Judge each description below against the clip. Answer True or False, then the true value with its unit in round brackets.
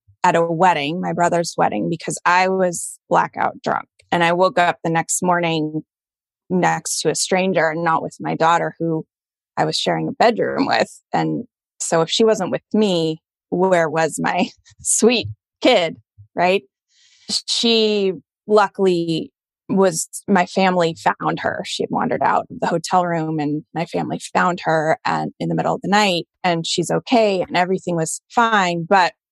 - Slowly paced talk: False (170 wpm)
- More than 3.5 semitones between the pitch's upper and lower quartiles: False (2.6 semitones)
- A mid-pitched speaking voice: True (175 Hz)